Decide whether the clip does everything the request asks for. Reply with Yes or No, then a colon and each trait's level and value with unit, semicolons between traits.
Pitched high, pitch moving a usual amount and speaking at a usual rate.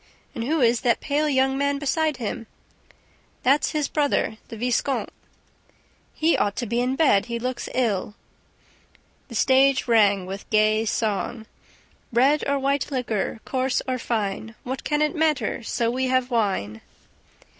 Yes: very high, 250 Hz; average, 3.9 semitones; average, 155 wpm